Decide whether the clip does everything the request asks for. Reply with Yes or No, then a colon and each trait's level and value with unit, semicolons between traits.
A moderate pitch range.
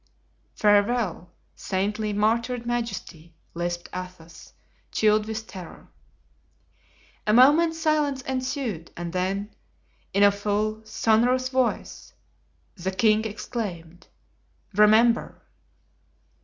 Yes: average, 4.3 semitones